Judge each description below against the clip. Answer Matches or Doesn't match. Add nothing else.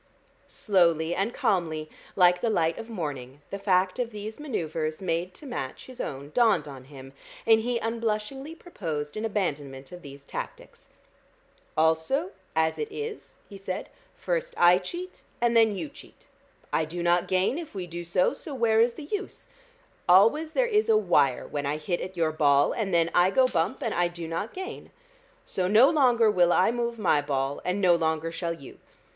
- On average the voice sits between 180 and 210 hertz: Matches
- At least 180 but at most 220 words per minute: Matches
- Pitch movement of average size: Doesn't match